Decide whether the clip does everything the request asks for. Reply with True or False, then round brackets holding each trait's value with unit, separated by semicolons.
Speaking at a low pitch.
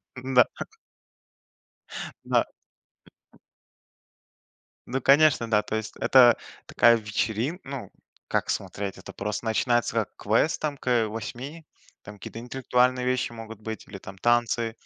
True (120 Hz)